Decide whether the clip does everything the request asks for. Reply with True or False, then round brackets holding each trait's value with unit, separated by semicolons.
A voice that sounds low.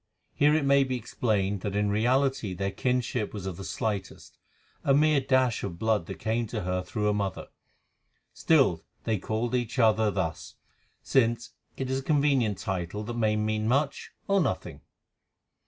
True (110 Hz)